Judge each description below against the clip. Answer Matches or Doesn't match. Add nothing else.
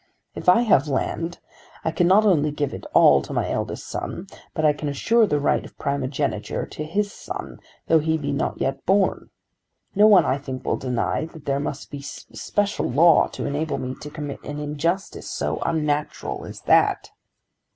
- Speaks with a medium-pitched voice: Matches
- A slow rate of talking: Doesn't match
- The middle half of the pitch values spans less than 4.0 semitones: Matches